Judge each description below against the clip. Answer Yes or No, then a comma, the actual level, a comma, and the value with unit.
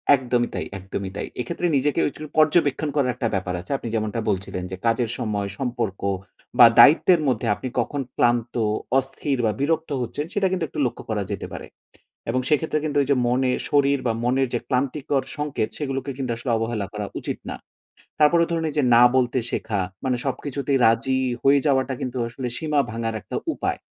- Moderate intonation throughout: Yes, average, 3.9 semitones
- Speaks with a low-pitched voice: Yes, low, 130 Hz